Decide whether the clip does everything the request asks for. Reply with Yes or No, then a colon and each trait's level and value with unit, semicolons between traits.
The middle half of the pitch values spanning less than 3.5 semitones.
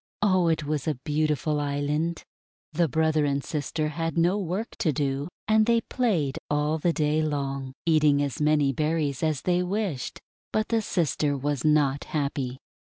Yes: average, 2.8 semitones